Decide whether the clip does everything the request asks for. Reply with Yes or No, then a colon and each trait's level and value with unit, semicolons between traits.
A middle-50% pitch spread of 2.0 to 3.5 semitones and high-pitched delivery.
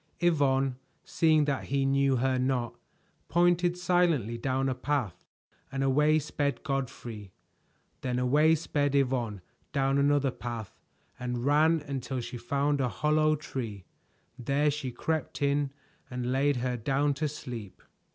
No: average, 2.9 semitones; low, 135 Hz